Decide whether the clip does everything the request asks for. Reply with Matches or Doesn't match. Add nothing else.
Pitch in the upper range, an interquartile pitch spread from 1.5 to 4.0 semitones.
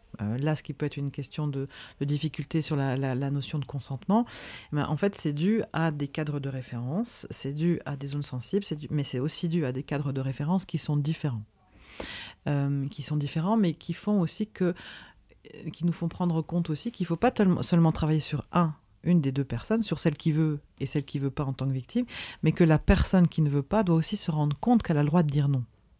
Doesn't match